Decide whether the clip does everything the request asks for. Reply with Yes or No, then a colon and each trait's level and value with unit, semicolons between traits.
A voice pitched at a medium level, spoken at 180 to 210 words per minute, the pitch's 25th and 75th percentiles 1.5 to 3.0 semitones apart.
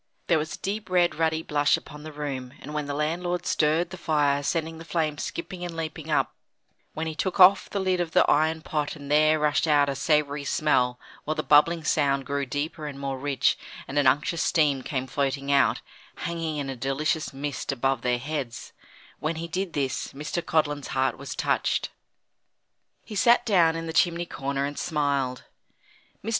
Yes: medium, 150 Hz; average, 190 wpm; average, 2.7 semitones